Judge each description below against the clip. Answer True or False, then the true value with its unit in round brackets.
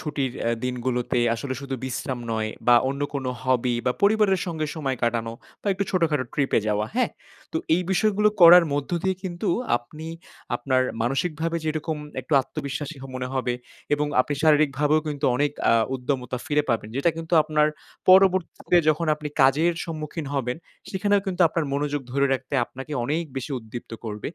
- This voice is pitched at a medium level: True (145 Hz)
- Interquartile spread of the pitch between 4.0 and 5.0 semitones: True (4.3 semitones)